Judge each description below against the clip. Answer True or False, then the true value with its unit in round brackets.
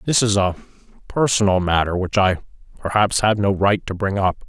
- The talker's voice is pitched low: True (100 Hz)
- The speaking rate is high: False (190 wpm)